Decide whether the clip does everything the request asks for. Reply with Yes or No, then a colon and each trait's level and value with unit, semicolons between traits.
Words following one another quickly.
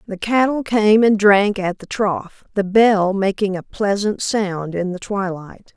No: average, 175 wpm